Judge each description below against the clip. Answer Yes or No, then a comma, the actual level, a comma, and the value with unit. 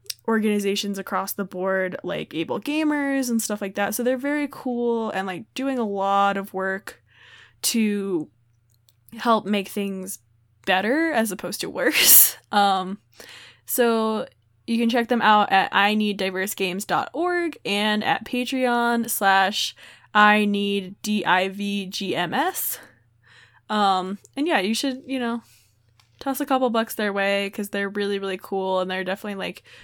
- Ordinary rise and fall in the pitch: Yes, average, 3.6 semitones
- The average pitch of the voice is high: Yes, high, 200 Hz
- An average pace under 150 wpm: Yes, slow, 135 wpm